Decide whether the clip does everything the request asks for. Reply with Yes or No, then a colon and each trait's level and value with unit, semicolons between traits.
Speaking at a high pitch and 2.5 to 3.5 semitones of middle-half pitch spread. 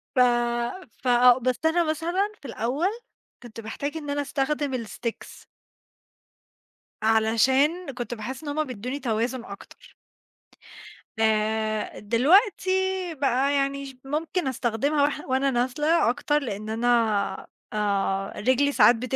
No: very high, 260 Hz; average, 4.3 semitones